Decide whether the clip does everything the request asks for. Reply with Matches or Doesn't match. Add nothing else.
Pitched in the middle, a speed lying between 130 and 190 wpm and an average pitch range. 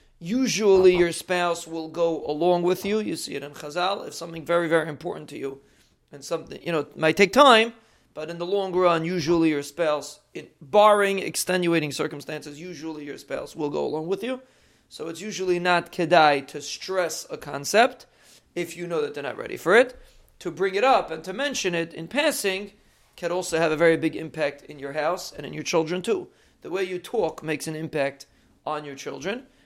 Doesn't match